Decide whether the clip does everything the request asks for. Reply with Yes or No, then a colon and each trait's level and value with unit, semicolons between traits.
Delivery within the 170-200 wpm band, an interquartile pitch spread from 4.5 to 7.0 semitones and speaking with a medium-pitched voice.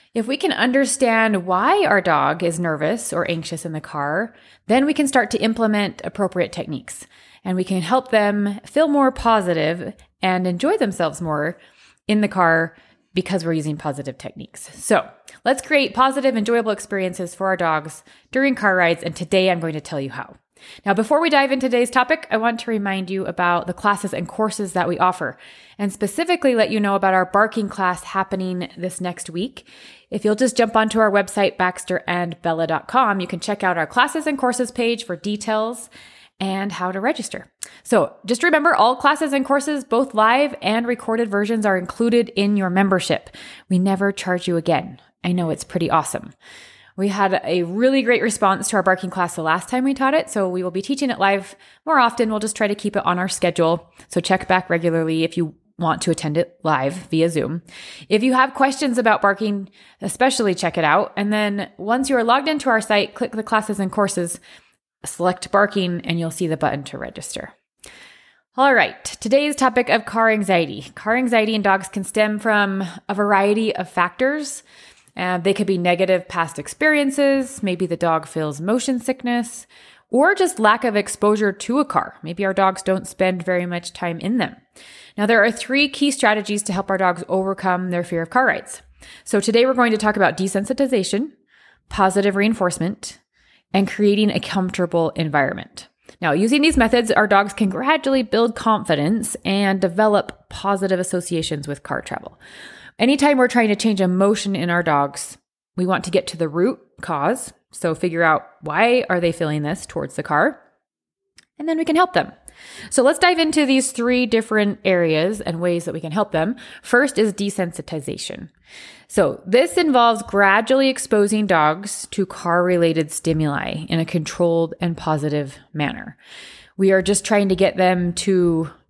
No: average, 185 wpm; average, 4.8 semitones; high, 200 Hz